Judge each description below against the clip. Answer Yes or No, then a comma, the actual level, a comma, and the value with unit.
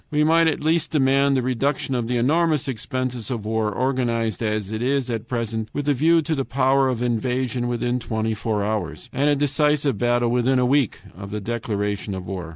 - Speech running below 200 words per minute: No, fast, 205 wpm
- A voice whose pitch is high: No, low, 125 Hz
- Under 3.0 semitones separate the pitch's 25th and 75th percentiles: No, average, 3.7 semitones